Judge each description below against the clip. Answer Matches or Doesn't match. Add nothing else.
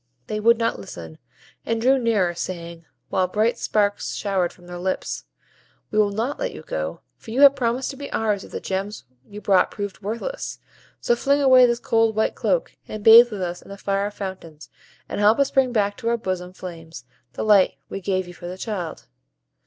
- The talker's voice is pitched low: Doesn't match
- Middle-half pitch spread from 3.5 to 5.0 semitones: Matches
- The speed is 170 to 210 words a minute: Matches